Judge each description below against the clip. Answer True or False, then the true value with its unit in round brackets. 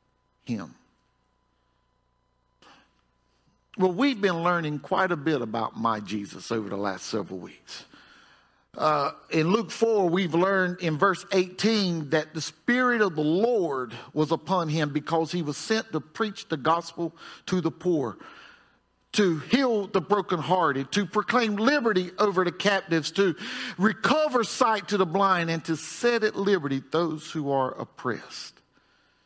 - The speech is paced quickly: False (145 wpm)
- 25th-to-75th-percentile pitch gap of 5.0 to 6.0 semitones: True (5.5 semitones)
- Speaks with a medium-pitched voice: True (175 Hz)